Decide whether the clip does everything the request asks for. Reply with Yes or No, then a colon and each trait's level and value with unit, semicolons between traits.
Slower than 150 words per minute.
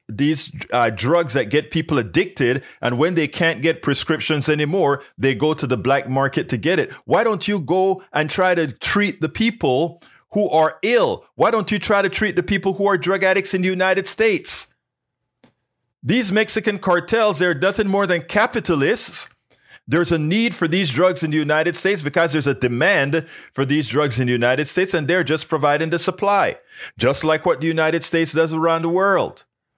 No: average, 195 wpm